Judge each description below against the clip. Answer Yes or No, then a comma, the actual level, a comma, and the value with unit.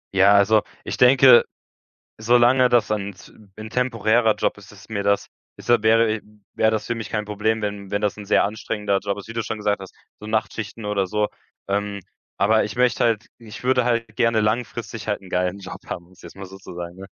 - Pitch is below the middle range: Yes, low, 105 Hz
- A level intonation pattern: Yes, narrow, 2.3 semitones